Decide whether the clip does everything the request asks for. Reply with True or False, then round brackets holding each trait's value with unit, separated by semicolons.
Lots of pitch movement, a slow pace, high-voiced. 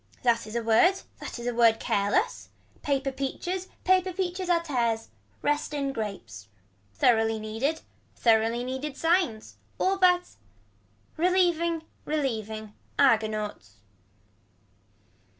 True (7.4 semitones; 110 wpm; 265 Hz)